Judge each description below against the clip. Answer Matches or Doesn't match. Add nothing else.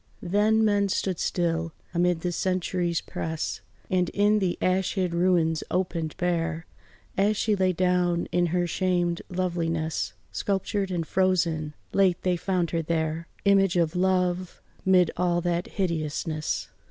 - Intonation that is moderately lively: Doesn't match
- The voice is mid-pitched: Matches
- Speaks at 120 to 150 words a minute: Matches